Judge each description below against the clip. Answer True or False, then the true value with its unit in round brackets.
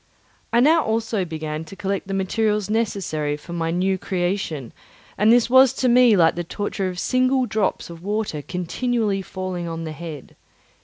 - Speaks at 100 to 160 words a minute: False (170 wpm)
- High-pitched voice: True (195 Hz)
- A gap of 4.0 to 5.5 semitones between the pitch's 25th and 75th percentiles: True (4.8 semitones)